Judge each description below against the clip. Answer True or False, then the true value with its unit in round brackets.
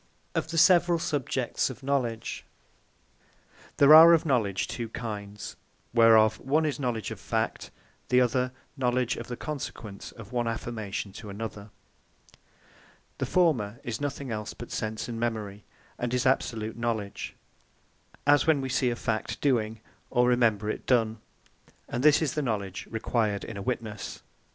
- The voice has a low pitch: True (120 Hz)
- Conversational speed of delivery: True (150 wpm)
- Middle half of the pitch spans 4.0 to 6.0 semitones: False (3.5 semitones)